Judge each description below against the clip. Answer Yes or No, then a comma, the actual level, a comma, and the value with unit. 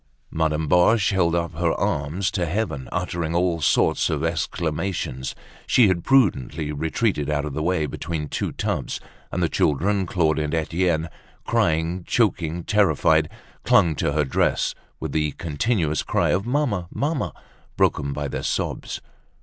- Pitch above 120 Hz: No, very low, 85 Hz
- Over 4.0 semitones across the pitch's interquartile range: No, average, 3.4 semitones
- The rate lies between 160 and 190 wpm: No, average, 150 wpm